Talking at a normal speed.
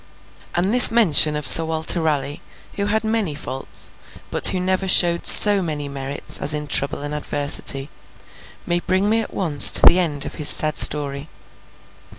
Yes: average, 170 wpm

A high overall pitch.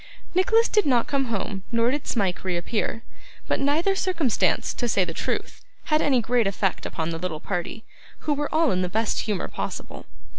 Yes: high, 230 Hz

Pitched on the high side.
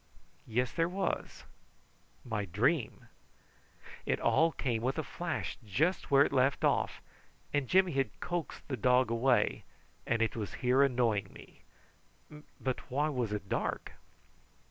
No: low, 130 Hz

